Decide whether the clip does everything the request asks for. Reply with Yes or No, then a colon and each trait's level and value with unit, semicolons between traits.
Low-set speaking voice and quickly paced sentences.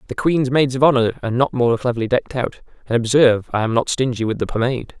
Yes: low, 125 Hz; fast, 240 wpm